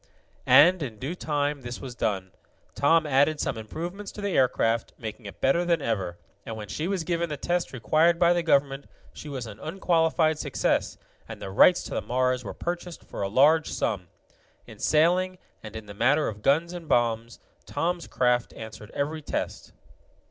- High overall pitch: No, medium, 145 Hz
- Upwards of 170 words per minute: Yes, average, 185 wpm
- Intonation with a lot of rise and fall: Yes, wide, 6.6 semitones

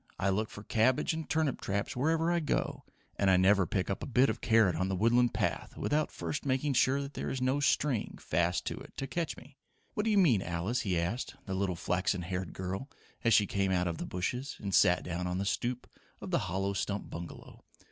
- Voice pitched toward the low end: Yes, low, 105 Hz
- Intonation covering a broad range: Yes, wide, 6.3 semitones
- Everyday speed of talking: No, fast, 225 wpm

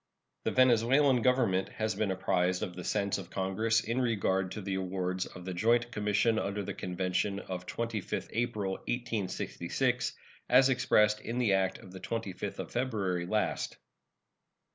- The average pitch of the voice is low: Yes, low, 105 Hz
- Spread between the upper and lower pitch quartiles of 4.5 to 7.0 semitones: No, average, 3.7 semitones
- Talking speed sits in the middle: Yes, average, 155 wpm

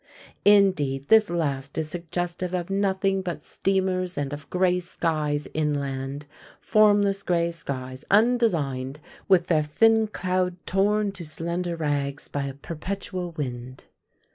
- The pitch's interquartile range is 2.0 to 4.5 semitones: No, average, 4.9 semitones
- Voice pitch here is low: No, medium, 170 Hz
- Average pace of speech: No, slow, 125 wpm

